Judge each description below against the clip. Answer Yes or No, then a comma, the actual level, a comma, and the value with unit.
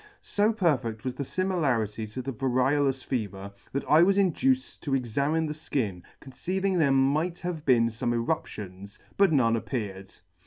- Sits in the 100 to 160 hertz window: Yes, low, 135 Hz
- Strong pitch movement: Yes, wide, 5.9 semitones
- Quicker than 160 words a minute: No, average, 155 wpm